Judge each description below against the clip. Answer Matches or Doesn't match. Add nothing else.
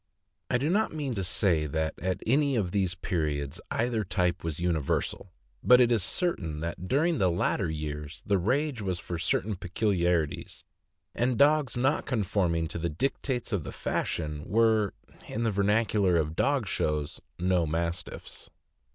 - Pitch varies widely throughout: Matches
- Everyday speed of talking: Matches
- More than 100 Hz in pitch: Doesn't match